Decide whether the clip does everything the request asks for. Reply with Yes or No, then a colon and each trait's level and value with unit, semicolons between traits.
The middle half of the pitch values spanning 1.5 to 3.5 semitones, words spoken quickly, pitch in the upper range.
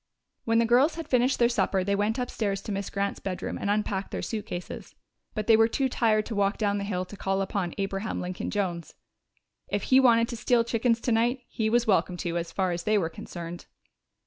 Yes: average, 3.2 semitones; fast, 215 wpm; high, 210 Hz